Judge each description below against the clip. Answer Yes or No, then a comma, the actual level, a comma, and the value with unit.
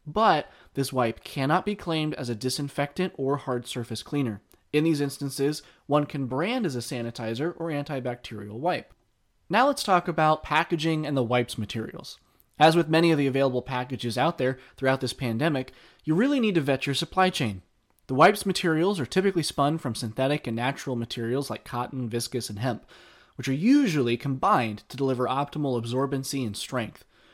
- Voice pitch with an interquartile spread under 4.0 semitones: No, average, 4.3 semitones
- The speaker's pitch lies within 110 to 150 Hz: Yes, low, 135 Hz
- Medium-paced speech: Yes, average, 175 wpm